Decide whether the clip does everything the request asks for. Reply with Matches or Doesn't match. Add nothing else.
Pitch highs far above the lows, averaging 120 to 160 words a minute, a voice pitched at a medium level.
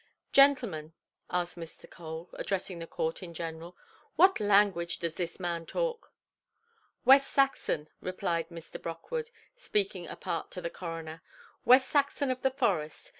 Matches